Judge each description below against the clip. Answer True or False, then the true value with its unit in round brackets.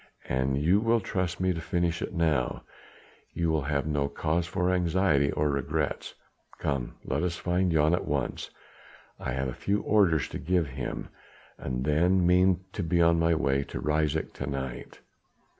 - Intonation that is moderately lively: True (4.2 semitones)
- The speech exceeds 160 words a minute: True (170 wpm)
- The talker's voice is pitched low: True (80 Hz)